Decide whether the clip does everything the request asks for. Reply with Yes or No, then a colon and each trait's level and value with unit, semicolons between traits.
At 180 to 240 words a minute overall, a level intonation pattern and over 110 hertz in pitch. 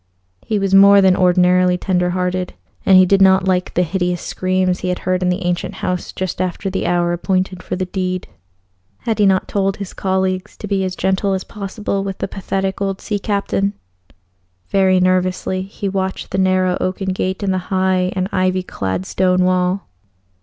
Yes: average, 190 wpm; narrow, 1.0 semitones; medium, 185 Hz